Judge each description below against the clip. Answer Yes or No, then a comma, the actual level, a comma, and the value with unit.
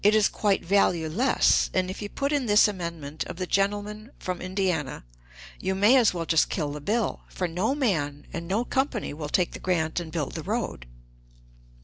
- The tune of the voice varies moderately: Yes, average, 4.3 semitones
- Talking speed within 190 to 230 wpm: Yes, average, 195 wpm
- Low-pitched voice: No, medium, 185 Hz